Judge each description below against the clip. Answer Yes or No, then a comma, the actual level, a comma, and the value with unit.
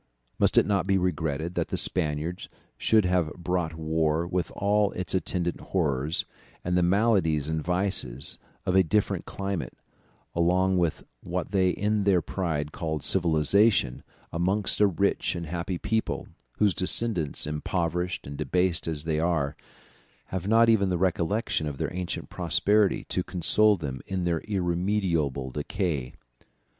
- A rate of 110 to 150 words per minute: Yes, average, 145 wpm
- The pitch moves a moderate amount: Yes, average, 3.4 semitones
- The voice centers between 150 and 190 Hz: No, very low, 90 Hz